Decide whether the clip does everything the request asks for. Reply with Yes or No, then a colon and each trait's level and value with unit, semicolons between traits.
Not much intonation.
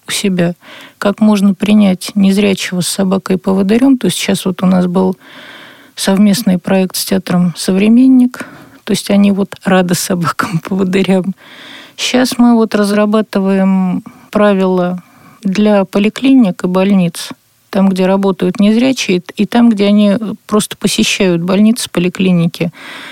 Yes: narrow, 2.3 semitones